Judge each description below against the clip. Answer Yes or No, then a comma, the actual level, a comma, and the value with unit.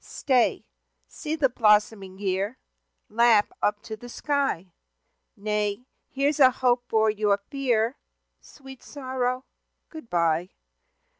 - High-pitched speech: Yes, high, 235 Hz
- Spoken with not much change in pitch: No, average, 4.1 semitones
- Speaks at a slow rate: Yes, slow, 115 wpm